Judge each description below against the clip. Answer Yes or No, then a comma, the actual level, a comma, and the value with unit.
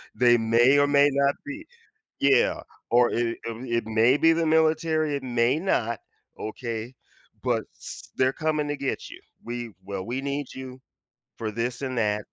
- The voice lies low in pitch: Yes, low, 130 Hz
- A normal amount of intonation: Yes, average, 3.5 semitones